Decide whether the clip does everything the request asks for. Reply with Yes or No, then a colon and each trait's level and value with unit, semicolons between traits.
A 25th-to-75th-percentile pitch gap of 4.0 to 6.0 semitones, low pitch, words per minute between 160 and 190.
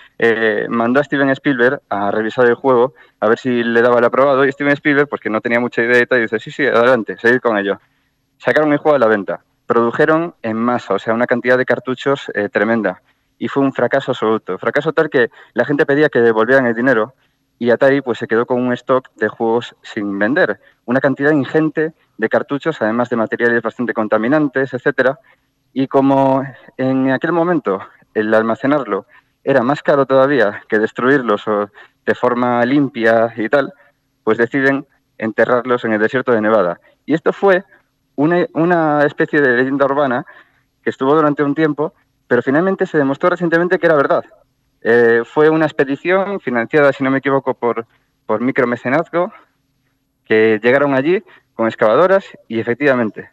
No: average, 3.6 semitones; low, 130 Hz; average, 175 wpm